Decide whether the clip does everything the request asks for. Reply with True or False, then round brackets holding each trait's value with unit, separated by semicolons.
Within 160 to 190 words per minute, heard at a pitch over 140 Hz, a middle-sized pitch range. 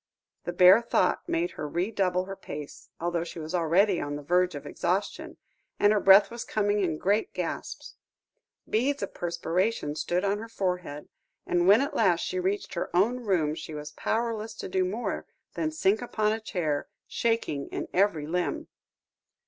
True (175 wpm; 185 Hz; 4.0 semitones)